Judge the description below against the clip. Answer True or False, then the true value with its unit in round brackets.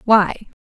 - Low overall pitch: False (205 Hz)